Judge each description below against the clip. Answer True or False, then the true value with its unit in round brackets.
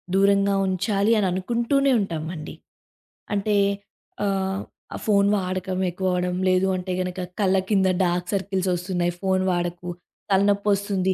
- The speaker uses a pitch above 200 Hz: False (190 Hz)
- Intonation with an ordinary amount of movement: False (1.6 semitones)